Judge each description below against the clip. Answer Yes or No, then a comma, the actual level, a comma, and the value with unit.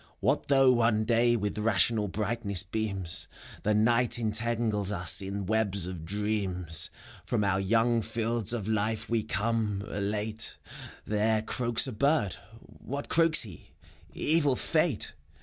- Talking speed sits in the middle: No, slow, 130 wpm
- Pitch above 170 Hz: No, low, 110 Hz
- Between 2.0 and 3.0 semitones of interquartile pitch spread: Yes, narrow, 2.6 semitones